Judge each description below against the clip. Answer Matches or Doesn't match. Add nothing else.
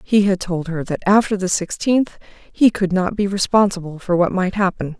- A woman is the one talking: Matches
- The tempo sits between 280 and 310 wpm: Doesn't match